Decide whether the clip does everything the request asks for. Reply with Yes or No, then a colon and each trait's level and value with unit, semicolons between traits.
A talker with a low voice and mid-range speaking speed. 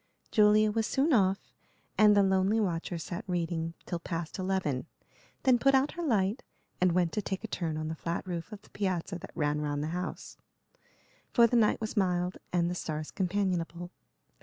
No: medium, 185 Hz; average, 185 wpm